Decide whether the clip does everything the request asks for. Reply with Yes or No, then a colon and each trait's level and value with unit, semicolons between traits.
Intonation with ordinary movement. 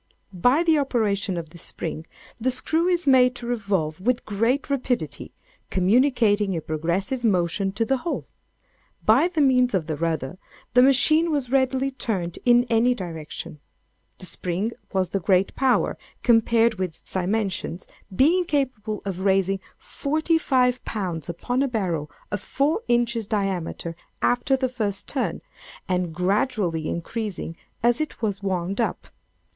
No: wide, 5.8 semitones